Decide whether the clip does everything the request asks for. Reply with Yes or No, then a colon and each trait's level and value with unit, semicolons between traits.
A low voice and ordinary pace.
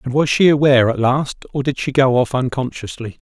No: low, 130 Hz; fast, 220 wpm